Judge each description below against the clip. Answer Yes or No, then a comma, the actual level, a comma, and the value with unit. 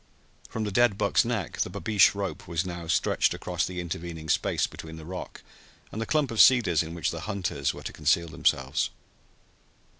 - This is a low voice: Yes, very low, 90 Hz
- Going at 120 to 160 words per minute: No, average, 185 wpm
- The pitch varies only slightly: No, average, 4.6 semitones